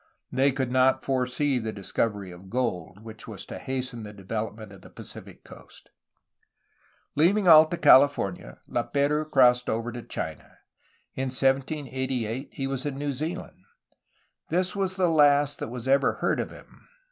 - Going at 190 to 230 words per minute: No, average, 155 wpm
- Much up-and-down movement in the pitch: No, average, 4.2 semitones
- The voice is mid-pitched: No, low, 130 Hz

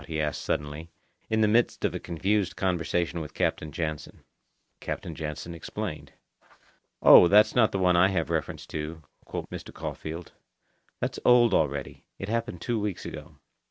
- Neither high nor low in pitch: No, very low, 85 Hz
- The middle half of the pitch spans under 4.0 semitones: No, average, 4.8 semitones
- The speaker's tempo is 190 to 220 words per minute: No, average, 160 wpm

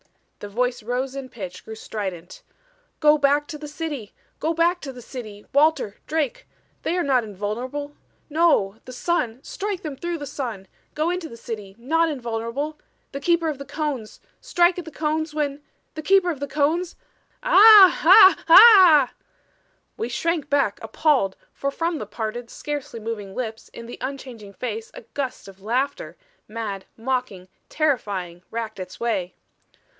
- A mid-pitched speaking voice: No, very high, 270 Hz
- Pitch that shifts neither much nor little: No, wide, 5.9 semitones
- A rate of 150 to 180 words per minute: Yes, average, 165 wpm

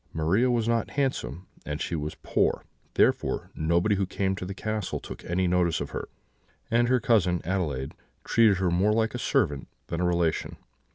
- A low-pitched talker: Yes, very low, 95 Hz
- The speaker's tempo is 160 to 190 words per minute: Yes, average, 180 wpm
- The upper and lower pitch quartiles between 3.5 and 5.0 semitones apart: Yes, average, 4.5 semitones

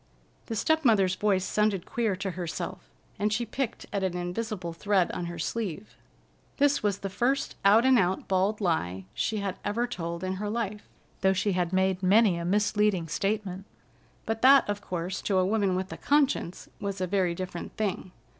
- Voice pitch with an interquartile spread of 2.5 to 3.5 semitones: Yes, average, 2.8 semitones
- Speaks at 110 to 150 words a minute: No, average, 185 wpm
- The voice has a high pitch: Yes, high, 195 Hz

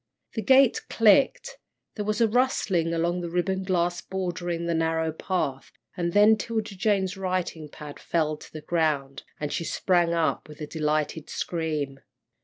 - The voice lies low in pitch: No, medium, 170 Hz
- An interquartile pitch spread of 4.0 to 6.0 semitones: No, average, 3.3 semitones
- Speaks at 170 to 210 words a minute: No, average, 160 wpm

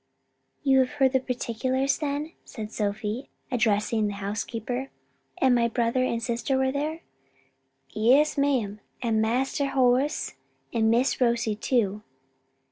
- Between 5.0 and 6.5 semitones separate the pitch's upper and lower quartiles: No, average, 3.3 semitones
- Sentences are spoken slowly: Yes, slow, 125 wpm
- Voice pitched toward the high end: Yes, high, 245 Hz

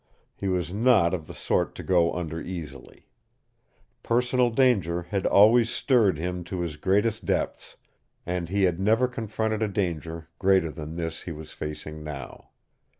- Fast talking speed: No, average, 155 wpm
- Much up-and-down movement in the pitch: No, average, 4.8 semitones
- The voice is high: No, very low, 90 Hz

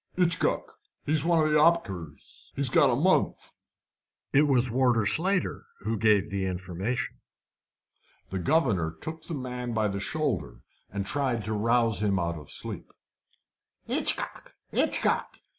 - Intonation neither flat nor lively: No, wide, 7.2 semitones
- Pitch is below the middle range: Yes, low, 115 Hz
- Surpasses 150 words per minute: No, average, 140 wpm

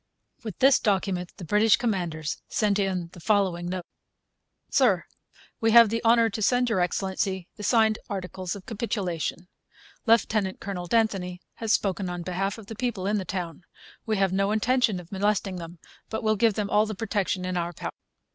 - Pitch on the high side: Yes, high, 195 Hz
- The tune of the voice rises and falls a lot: No, average, 3.3 semitones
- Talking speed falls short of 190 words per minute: Yes, average, 180 wpm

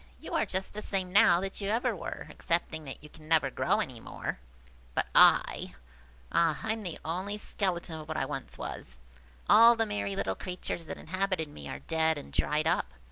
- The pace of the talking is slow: No, average, 200 wpm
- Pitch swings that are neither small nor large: Yes, average, 4.2 semitones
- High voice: No, medium, 170 Hz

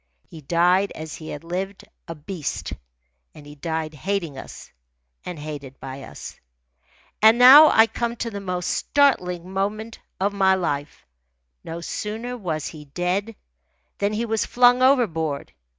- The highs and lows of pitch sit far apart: Yes, wide, 5.7 semitones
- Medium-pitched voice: Yes, medium, 180 Hz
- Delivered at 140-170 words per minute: Yes, average, 150 wpm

